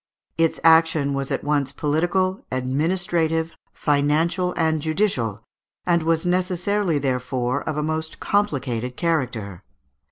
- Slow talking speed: Yes, slow, 115 wpm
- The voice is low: No, medium, 155 Hz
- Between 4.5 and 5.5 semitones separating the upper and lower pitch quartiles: No, average, 3.8 semitones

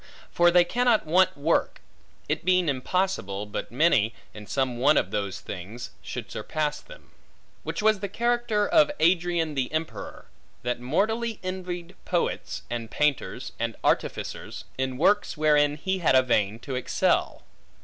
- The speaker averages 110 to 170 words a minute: Yes, average, 150 wpm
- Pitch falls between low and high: Yes, medium, 155 Hz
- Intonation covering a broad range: Yes, wide, 6.8 semitones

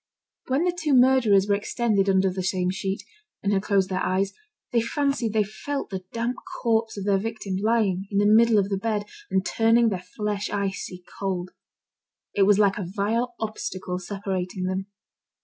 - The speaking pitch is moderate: No, high, 200 Hz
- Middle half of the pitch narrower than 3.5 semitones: Yes, average, 2.9 semitones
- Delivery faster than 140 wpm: Yes, average, 180 wpm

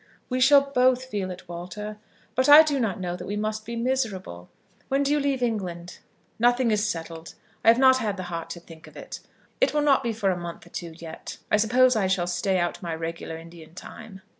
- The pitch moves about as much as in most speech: No, wide, 6.5 semitones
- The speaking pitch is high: Yes, high, 210 Hz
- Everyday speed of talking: No, fast, 225 wpm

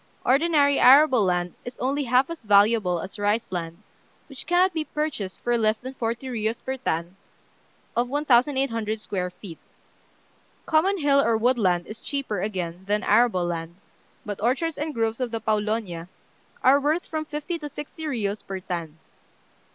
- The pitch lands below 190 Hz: No, high, 230 Hz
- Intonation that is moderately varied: No, wide, 5.9 semitones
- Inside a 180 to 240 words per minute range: No, average, 160 wpm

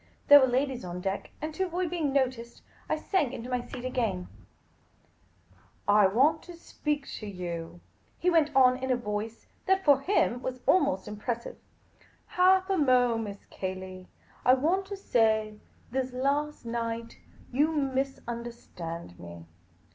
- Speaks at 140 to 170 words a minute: Yes, average, 160 wpm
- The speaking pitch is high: Yes, very high, 250 Hz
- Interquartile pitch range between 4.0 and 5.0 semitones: No, wide, 5.6 semitones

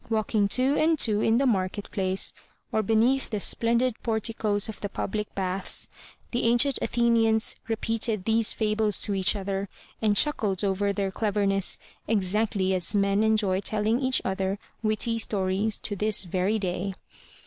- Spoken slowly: No, average, 155 wpm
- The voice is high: Yes, high, 210 Hz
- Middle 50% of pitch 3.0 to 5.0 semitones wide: No, narrow, 2.4 semitones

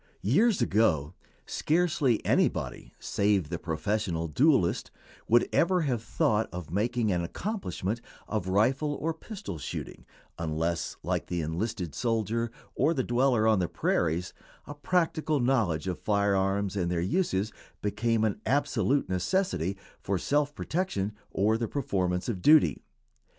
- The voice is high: No, low, 110 Hz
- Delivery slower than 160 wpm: Yes, average, 140 wpm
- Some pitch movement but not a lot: No, wide, 7.3 semitones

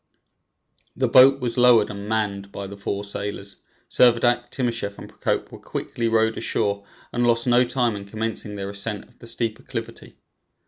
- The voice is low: Yes, low, 110 Hz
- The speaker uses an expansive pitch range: No, average, 3.1 semitones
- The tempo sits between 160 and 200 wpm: Yes, average, 170 wpm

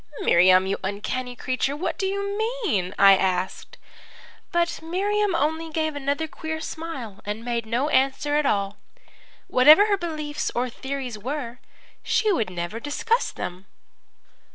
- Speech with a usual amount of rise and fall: No, wide, 7.4 semitones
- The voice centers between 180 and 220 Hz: No, very high, 280 Hz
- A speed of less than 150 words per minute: Yes, average, 140 wpm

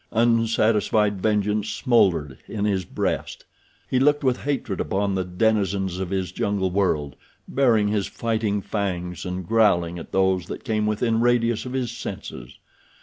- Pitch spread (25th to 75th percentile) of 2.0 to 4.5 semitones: Yes, average, 3.4 semitones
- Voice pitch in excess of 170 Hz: No, low, 105 Hz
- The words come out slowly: No, average, 145 wpm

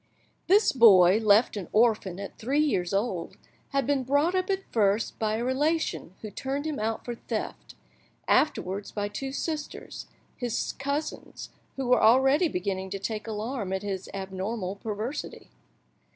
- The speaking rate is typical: Yes, average, 150 wpm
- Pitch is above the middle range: Yes, high, 225 Hz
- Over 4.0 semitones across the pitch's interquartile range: Yes, wide, 5.6 semitones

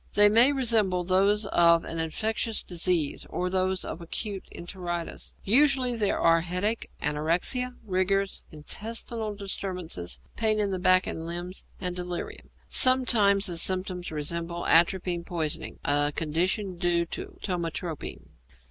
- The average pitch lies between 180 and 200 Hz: Yes, medium, 185 Hz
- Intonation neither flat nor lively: Yes, average, 3.6 semitones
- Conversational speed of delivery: No, slow, 130 wpm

